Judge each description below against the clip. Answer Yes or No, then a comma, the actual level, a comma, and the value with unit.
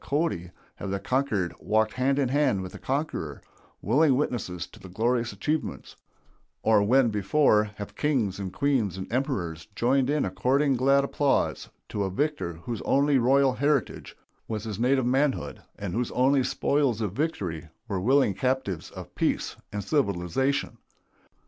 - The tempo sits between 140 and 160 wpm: Yes, average, 155 wpm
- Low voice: Yes, low, 125 Hz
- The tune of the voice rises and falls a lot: Yes, wide, 5.7 semitones